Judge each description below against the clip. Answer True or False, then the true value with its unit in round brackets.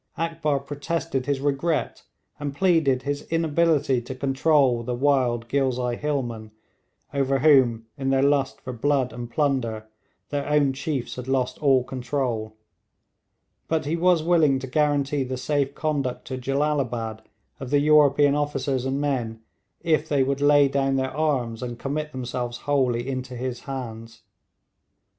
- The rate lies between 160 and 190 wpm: False (145 wpm)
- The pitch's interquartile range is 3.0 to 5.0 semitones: False (2.6 semitones)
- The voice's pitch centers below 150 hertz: True (135 Hz)